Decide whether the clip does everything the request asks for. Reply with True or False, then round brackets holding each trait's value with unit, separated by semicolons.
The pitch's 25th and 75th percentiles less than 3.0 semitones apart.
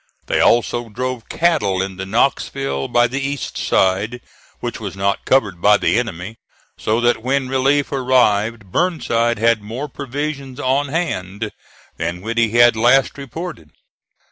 False (4.7 semitones)